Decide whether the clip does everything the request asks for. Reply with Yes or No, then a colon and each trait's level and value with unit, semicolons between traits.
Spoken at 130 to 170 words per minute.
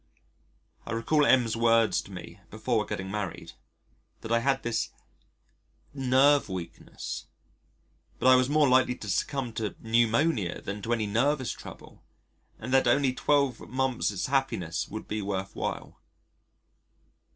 Yes: average, 140 wpm